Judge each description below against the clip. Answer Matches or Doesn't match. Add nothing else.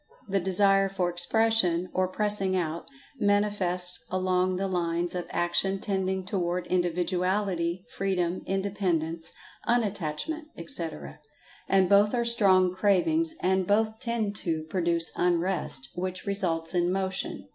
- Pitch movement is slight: Matches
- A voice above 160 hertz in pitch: Matches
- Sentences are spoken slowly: Matches